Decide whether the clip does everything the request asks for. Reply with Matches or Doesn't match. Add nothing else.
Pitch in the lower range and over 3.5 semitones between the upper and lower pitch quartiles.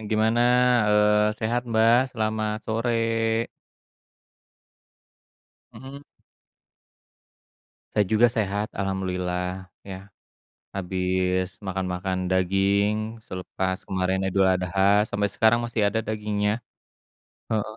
Doesn't match